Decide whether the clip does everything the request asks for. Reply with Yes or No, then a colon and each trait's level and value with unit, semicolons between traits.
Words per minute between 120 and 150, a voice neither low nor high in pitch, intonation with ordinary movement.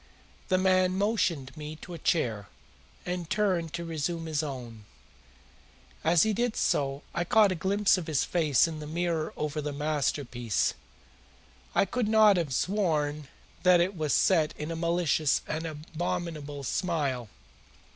Yes: average, 145 wpm; medium, 165 Hz; average, 3.6 semitones